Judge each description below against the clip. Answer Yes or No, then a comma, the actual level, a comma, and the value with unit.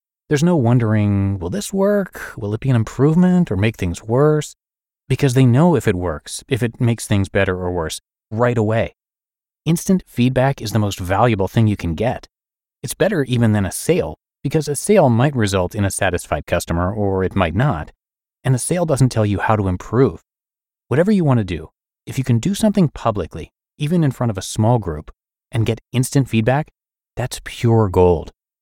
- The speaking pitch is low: Yes, low, 115 Hz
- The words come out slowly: No, average, 195 wpm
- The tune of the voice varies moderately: No, wide, 5.9 semitones